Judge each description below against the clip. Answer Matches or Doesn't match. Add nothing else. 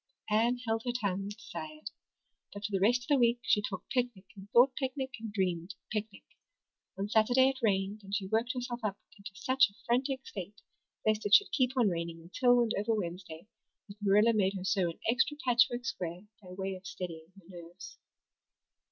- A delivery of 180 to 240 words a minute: Matches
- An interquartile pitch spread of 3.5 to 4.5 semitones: Matches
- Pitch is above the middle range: Matches